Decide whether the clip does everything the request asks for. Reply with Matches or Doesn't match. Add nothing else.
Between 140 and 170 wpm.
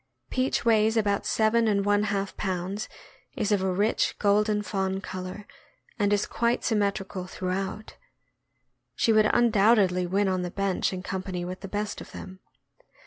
Matches